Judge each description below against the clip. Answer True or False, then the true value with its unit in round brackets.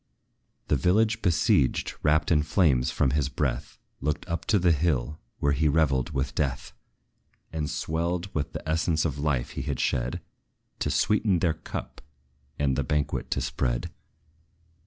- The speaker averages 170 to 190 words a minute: False (155 wpm)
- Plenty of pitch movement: False (3.7 semitones)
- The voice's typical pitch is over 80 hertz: False (75 Hz)